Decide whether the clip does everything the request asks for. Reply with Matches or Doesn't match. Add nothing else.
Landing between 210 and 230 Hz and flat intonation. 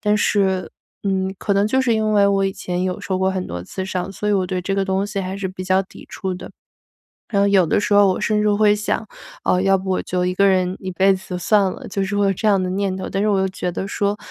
Doesn't match